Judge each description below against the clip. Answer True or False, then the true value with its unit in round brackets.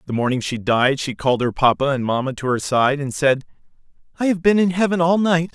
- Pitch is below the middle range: False (145 Hz)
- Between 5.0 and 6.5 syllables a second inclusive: True (5.8 syllables/s)